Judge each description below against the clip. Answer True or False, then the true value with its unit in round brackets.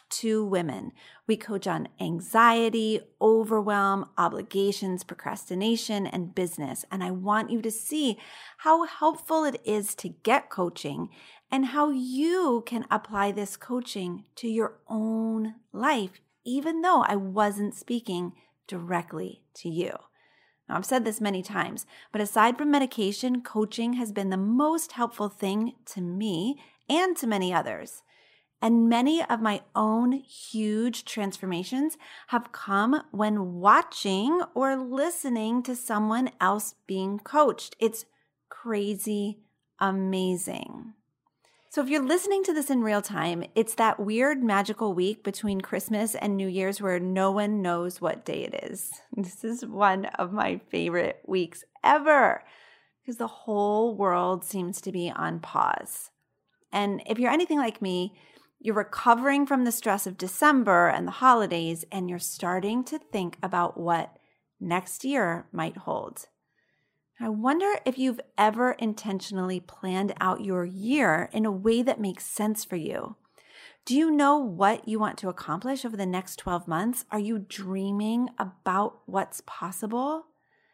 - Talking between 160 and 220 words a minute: False (145 wpm)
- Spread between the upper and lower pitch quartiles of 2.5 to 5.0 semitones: True (4.6 semitones)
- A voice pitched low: False (215 Hz)